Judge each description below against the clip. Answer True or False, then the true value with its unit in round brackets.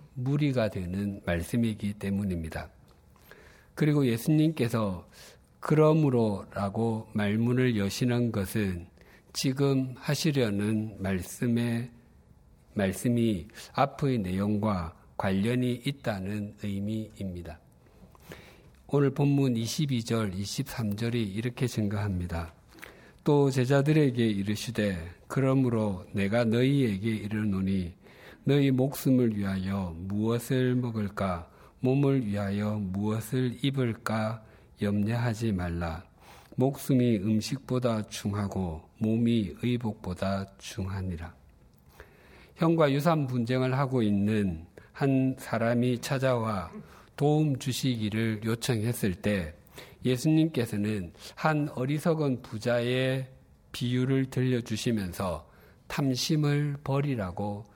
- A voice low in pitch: True (115 Hz)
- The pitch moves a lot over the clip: False (4.6 semitones)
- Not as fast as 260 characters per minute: True (220 characters per minute)